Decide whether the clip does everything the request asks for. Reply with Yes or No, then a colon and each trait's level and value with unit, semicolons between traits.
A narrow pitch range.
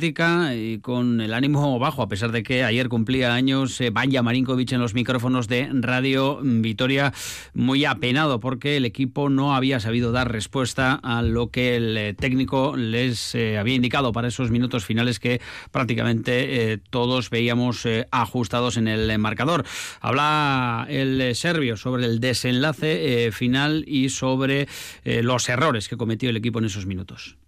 Yes: narrow, 2.2 semitones